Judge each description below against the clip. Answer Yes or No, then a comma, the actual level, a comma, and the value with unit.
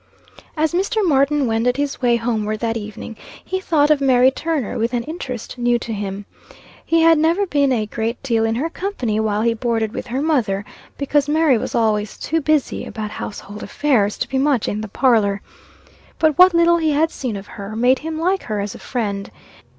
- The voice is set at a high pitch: Yes, very high, 250 Hz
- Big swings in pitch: Yes, wide, 5.8 semitones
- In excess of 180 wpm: Yes, average, 200 wpm